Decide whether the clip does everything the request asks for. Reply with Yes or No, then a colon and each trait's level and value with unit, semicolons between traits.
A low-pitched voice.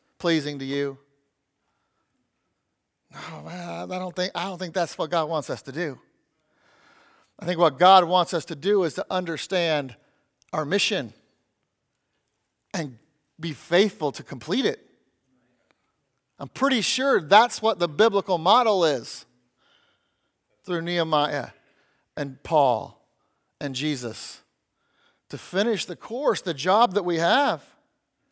No: medium, 170 Hz